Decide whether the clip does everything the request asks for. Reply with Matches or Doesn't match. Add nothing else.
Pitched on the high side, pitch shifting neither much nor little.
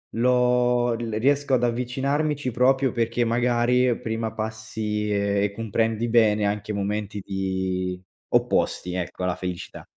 Doesn't match